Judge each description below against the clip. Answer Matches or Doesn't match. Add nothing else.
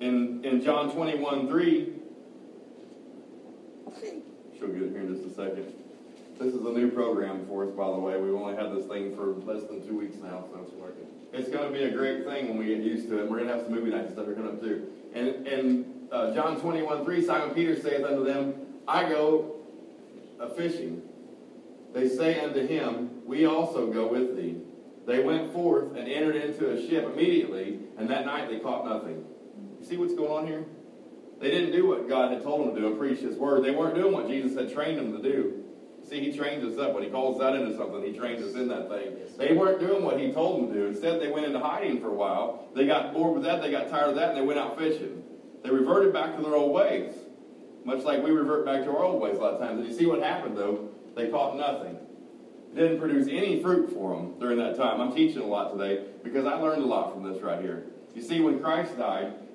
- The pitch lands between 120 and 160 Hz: Matches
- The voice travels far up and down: Matches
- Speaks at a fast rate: Matches